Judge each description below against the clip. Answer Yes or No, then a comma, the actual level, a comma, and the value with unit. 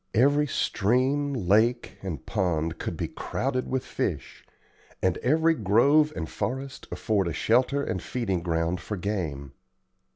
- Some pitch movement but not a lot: No, wide, 7.0 semitones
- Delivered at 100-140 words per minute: Yes, slow, 135 wpm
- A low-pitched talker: Yes, low, 110 Hz